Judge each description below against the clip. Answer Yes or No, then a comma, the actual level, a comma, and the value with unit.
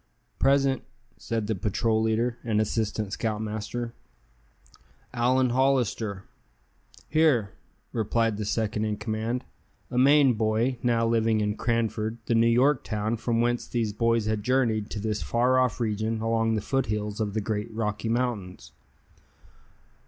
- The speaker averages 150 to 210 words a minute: No, average, 140 wpm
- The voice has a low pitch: Yes, low, 115 Hz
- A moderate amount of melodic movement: No, narrow, 2.0 semitones